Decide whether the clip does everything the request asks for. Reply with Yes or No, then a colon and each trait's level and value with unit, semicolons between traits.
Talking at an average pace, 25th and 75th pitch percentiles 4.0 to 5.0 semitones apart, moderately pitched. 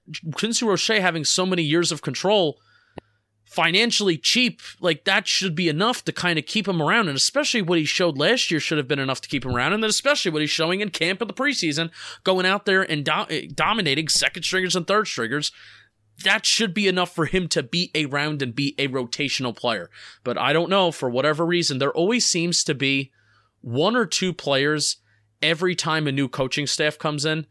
No: fast, 210 wpm; average, 4.7 semitones; medium, 165 Hz